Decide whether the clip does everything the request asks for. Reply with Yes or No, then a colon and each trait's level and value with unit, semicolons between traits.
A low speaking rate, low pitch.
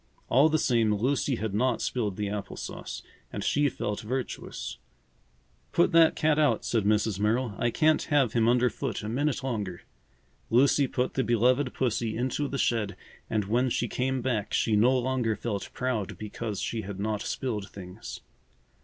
No: average, 170 wpm; low, 120 Hz